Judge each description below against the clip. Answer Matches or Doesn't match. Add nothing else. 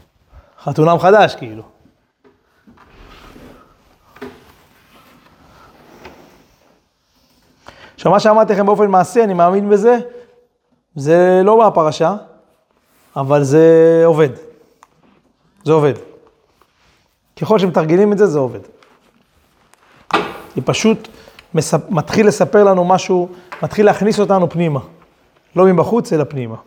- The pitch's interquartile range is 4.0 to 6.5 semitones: Matches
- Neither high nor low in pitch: Matches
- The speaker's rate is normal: Doesn't match